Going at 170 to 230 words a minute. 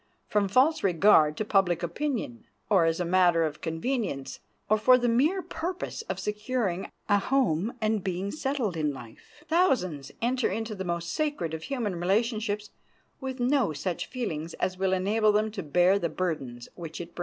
Yes: average, 175 wpm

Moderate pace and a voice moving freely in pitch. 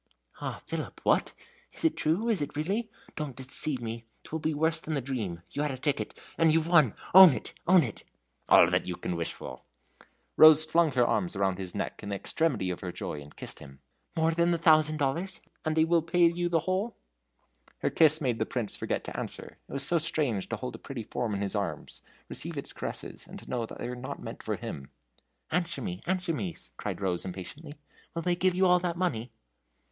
No: fast, 215 wpm; wide, 6.6 semitones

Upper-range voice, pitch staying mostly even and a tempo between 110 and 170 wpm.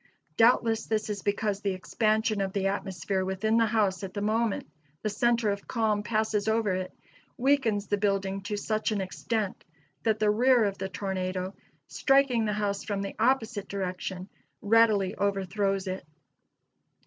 Yes: high, 205 Hz; narrow, 2.2 semitones; average, 160 wpm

